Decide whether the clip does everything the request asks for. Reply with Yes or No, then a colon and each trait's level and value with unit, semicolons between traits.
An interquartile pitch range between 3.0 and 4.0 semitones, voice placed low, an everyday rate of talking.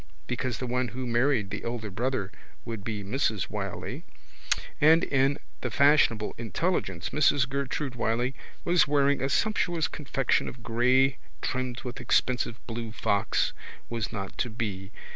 Yes: average, 3.4 semitones; low, 125 Hz; average, 145 wpm